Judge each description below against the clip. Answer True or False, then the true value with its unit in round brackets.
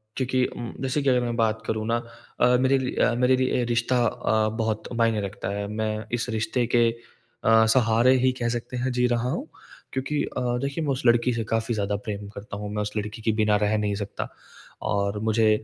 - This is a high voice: False (115 Hz)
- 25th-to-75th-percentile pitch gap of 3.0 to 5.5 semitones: False (2.6 semitones)